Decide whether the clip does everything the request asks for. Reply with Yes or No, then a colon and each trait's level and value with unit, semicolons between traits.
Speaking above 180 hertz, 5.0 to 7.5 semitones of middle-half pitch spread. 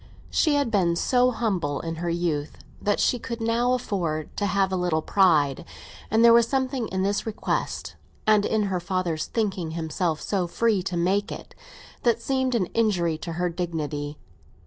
Yes: high, 190 Hz; average, 5.3 semitones